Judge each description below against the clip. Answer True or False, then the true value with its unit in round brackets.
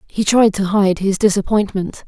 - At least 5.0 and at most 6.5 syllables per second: False (4.7 syllables/s)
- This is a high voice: True (200 Hz)